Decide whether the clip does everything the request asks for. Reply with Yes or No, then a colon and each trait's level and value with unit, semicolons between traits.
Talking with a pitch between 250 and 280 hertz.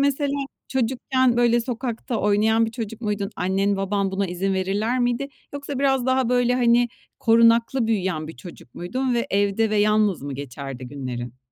No: high, 220 Hz